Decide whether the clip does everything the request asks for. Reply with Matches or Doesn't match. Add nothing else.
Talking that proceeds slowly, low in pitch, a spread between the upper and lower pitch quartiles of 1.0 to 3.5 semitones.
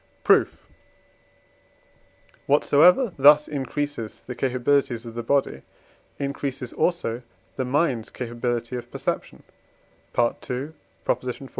Matches